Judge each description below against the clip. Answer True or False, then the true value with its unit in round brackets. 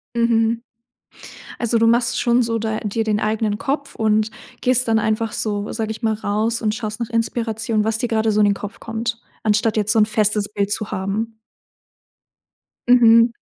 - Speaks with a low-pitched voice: False (220 Hz)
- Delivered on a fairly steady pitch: True (1.4 semitones)